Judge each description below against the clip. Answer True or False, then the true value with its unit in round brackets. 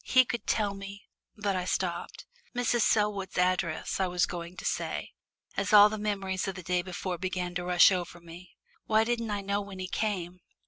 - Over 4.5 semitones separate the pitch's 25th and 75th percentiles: False (2.5 semitones)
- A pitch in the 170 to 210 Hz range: True (190 Hz)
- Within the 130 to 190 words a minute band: False (200 wpm)